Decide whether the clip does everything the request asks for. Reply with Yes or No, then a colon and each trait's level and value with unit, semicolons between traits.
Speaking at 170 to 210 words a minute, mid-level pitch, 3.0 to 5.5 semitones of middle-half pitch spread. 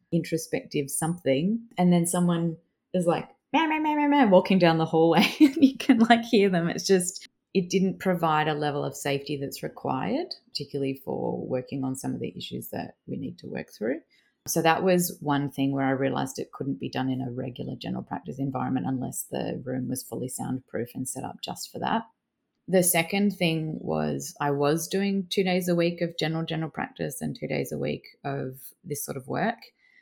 Yes: average, 200 wpm; medium, 170 Hz; average, 5.1 semitones